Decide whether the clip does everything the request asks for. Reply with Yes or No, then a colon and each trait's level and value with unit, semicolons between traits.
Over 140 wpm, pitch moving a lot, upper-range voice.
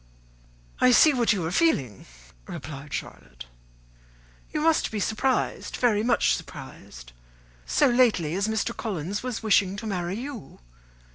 No: slow, 135 wpm; wide, 6.3 semitones; high, 210 Hz